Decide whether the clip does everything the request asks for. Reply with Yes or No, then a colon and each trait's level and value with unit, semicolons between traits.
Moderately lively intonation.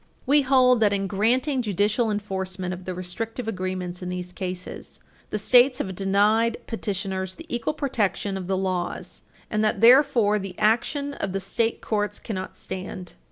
Yes: average, 3.7 semitones